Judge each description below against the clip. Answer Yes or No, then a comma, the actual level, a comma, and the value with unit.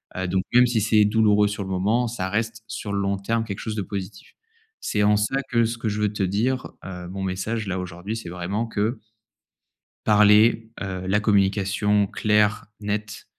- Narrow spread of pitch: Yes, narrow, 2.3 semitones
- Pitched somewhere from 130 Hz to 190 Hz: No, low, 105 Hz